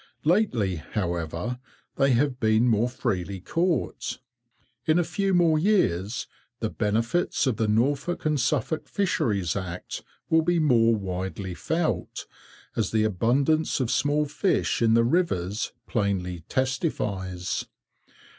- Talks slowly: Yes, slow, 125 wpm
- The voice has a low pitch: Yes, low, 120 Hz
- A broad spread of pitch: Yes, wide, 7.7 semitones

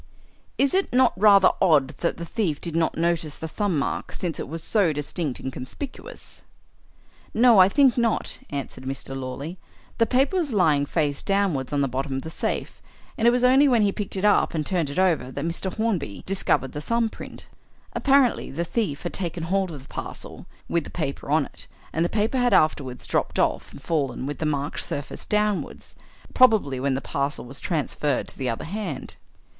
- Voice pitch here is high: No, medium, 170 Hz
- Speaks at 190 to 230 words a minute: Yes, average, 200 wpm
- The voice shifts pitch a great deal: Yes, wide, 6.9 semitones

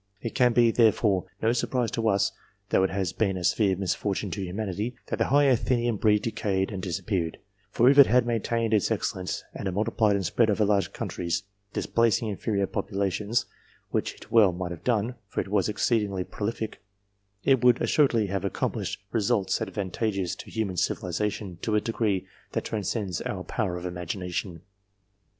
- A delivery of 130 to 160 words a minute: No, average, 180 wpm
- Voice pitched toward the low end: Yes, low, 105 Hz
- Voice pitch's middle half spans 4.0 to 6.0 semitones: No, average, 3.2 semitones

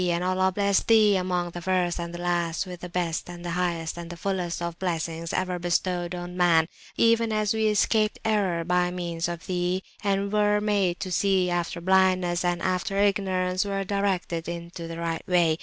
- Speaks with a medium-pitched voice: Yes, medium, 180 Hz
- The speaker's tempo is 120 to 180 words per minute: No, average, 190 wpm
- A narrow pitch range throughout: Yes, narrow, 2.1 semitones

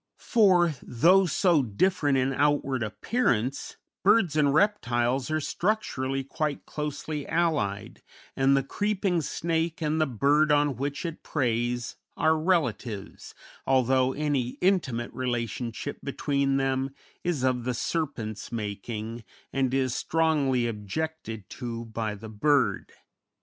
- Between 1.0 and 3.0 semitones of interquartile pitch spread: No, average, 4.8 semitones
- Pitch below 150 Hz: Yes, low, 135 Hz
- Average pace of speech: No, slow, 120 wpm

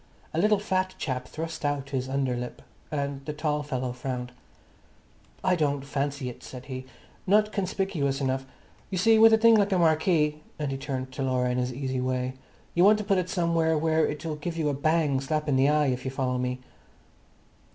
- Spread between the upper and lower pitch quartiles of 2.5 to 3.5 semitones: No, average, 4.2 semitones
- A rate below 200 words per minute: No, fast, 205 wpm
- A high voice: No, medium, 145 Hz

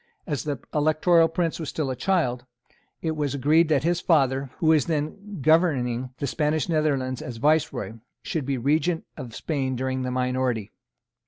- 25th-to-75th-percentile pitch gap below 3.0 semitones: No, average, 3.7 semitones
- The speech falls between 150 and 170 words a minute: Yes, average, 165 wpm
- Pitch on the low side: No, medium, 145 Hz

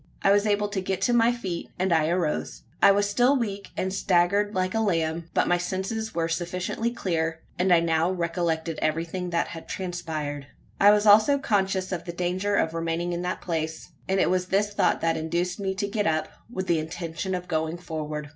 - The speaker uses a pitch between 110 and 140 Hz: No, medium, 180 Hz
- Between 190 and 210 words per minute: Yes, fast, 205 wpm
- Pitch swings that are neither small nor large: Yes, average, 3.3 semitones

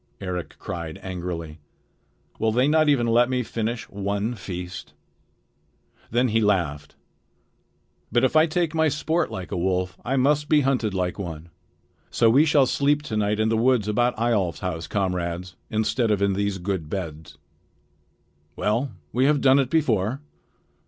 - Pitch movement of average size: No, wide, 6.1 semitones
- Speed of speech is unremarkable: Yes, average, 160 wpm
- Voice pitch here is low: Yes, low, 110 Hz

